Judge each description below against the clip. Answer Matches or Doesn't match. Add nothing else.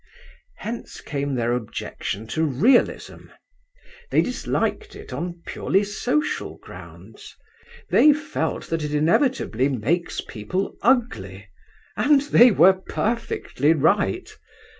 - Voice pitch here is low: Doesn't match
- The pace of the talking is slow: Matches